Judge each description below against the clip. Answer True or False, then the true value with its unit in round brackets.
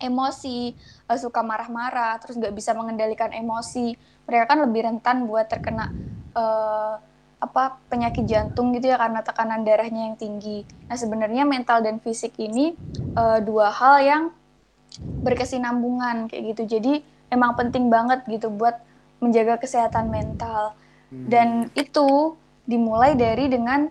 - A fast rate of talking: False (130 wpm)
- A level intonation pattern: True (2.1 semitones)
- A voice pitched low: False (235 Hz)